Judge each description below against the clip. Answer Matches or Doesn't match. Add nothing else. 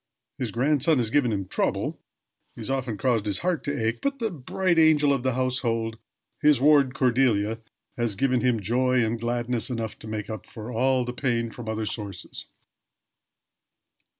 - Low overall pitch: Matches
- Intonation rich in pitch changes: Doesn't match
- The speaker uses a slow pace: Doesn't match